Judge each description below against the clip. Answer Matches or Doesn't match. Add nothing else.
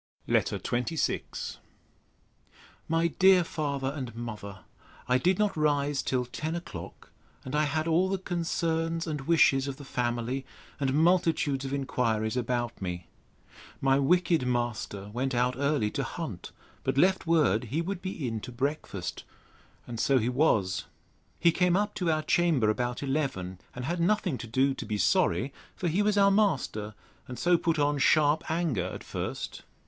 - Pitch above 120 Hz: Matches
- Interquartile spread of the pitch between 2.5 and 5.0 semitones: Doesn't match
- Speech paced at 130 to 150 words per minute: Doesn't match